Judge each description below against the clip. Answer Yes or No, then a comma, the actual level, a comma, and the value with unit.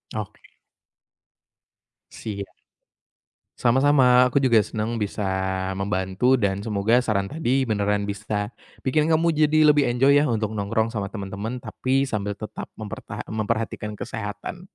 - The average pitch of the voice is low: Yes, low, 110 Hz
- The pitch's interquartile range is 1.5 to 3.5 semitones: No, average, 4.0 semitones